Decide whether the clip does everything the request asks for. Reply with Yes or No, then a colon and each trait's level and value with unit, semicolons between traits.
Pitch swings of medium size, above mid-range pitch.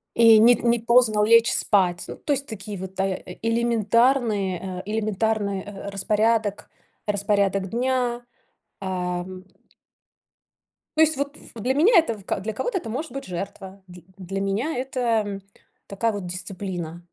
Yes: average, 3.6 semitones; high, 210 Hz